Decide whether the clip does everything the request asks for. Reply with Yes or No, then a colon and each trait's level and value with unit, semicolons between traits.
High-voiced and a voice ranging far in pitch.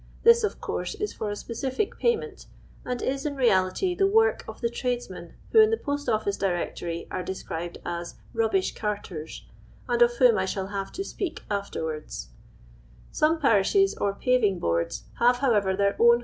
Yes: high, 230 Hz; wide, 7.1 semitones